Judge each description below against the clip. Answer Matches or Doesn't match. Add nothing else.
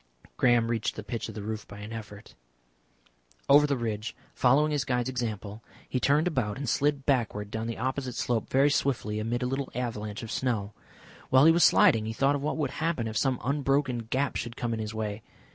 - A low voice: Matches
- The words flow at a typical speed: Doesn't match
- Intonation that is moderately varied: Matches